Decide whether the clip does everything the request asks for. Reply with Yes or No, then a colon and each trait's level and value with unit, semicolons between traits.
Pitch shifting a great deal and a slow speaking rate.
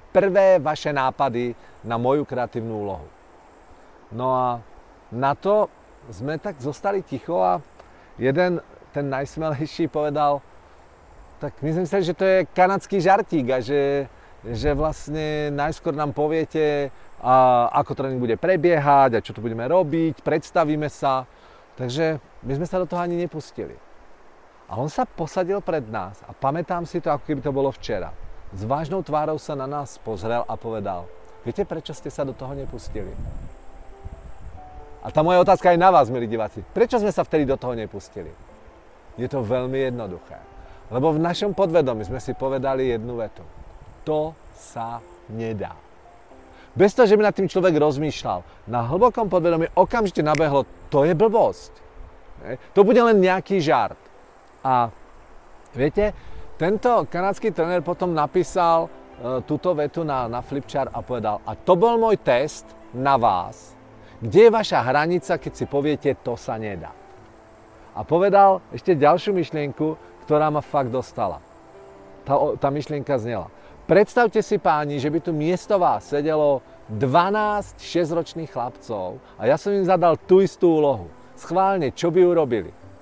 No: wide, 6.8 semitones; average, 150 wpm